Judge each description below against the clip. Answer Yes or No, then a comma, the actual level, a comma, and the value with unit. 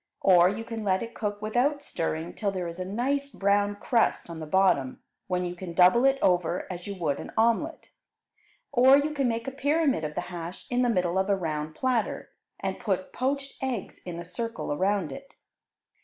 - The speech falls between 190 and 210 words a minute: Yes, average, 200 wpm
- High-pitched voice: Yes, high, 200 Hz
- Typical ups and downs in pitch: No, wide, 5.8 semitones